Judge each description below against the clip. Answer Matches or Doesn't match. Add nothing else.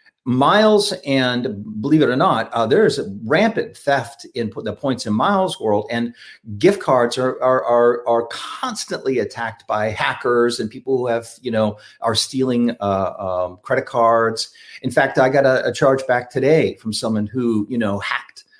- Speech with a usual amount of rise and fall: Matches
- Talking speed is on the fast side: Doesn't match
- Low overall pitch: Matches